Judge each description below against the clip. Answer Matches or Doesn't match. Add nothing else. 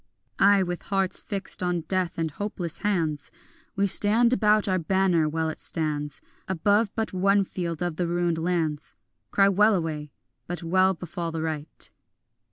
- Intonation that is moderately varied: Matches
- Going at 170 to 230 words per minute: Doesn't match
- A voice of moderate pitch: Matches